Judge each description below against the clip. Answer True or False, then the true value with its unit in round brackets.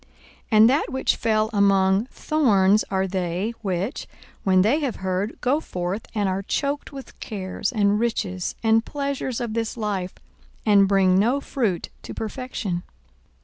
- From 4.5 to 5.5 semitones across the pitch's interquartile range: False (4.0 semitones)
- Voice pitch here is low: False (210 Hz)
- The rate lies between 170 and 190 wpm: False (150 wpm)